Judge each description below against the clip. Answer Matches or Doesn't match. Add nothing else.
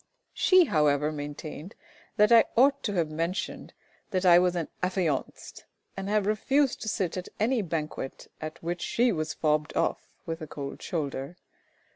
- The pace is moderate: Matches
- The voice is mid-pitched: Matches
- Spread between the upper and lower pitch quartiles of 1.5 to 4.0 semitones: Doesn't match